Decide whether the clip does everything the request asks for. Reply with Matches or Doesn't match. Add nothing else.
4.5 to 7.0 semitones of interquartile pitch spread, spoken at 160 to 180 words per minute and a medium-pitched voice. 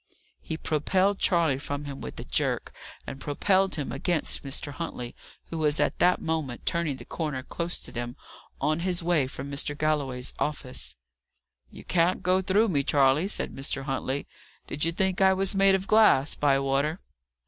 Matches